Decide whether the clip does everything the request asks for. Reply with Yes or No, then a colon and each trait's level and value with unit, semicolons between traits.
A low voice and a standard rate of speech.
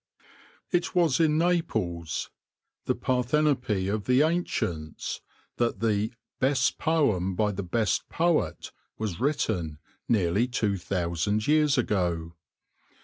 No: low, 110 Hz; slow, 130 wpm